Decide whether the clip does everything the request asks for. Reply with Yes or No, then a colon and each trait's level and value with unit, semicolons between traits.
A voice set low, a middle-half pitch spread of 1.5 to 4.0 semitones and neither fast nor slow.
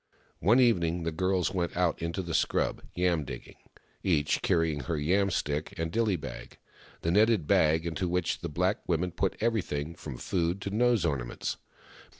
Yes: very low, 85 Hz; average, 2.9 semitones; average, 175 wpm